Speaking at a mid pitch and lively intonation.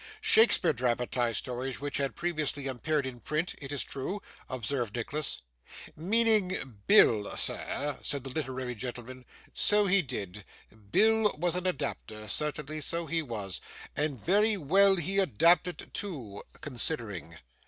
Yes: medium, 145 Hz; wide, 6.3 semitones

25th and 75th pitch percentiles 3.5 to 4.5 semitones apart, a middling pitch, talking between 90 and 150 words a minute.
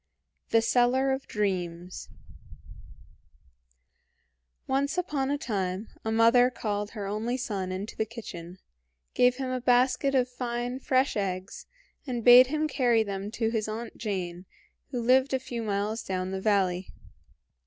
No: average, 4.2 semitones; high, 230 Hz; average, 145 wpm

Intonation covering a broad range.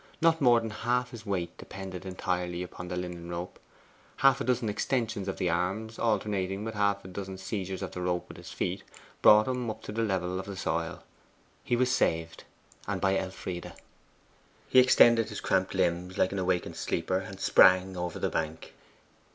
No: average, 3.5 semitones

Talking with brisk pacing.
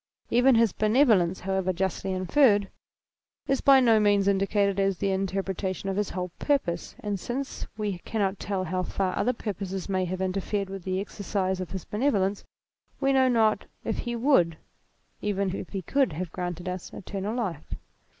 No: average, 170 wpm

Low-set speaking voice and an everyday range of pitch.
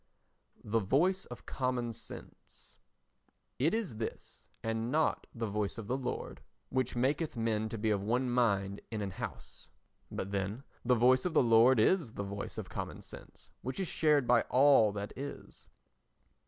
Yes: low, 120 Hz; average, 3.5 semitones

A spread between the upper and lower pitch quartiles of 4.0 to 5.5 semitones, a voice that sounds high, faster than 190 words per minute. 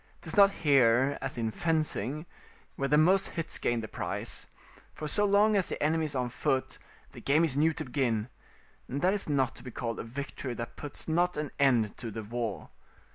No: average, 5.1 semitones; medium, 140 Hz; fast, 205 wpm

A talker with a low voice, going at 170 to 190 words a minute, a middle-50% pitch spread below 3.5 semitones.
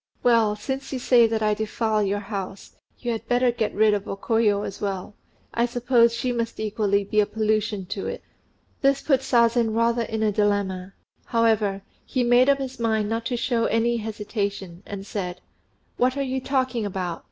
No: high, 220 Hz; average, 185 wpm; average, 2.8 semitones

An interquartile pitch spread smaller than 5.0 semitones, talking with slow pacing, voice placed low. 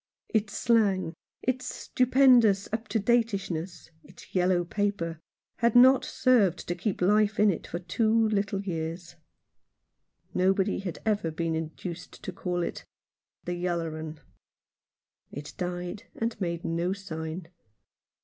No: average, 4.1 semitones; slow, 130 wpm; high, 190 Hz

